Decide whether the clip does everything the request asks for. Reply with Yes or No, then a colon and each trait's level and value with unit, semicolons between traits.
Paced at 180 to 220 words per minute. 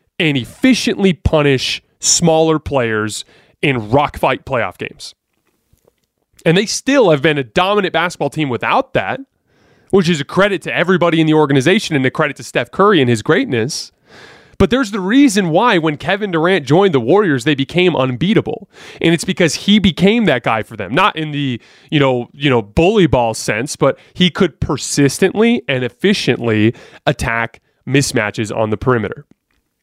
No: average, 165 wpm